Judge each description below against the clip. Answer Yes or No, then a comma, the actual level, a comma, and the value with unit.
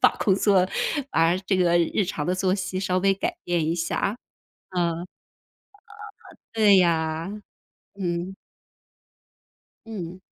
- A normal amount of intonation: No, narrow, 2.1 semitones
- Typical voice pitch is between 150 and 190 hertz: Yes, medium, 185 Hz